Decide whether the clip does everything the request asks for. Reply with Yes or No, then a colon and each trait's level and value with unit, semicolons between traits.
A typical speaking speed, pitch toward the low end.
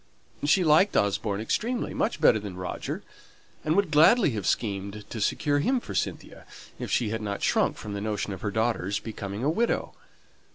Yes: average, 180 wpm; low, 110 Hz